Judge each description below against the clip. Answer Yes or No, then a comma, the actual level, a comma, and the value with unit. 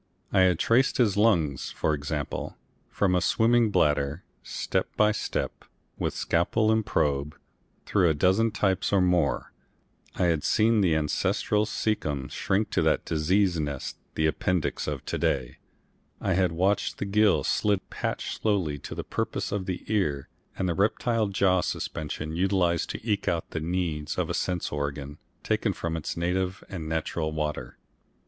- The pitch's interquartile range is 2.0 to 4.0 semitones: No, average, 4.7 semitones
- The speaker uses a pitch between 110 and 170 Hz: No, very low, 90 Hz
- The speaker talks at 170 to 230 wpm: No, average, 160 wpm